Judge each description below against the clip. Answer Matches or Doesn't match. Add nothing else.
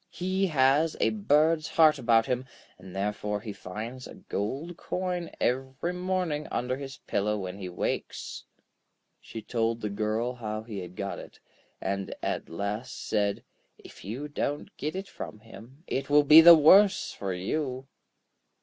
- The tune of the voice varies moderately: Doesn't match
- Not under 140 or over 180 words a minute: Matches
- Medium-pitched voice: Doesn't match